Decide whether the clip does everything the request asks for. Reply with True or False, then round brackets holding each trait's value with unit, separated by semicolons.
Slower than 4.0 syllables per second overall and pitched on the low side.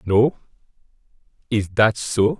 True (3.3 syllables/s; 105 Hz)